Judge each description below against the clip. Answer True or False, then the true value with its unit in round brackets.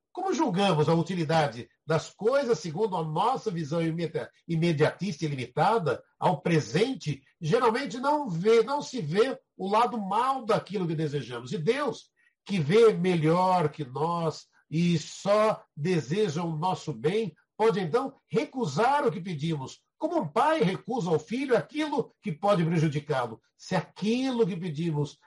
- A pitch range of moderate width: False (6.1 semitones)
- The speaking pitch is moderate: True (180 Hz)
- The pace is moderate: True (145 wpm)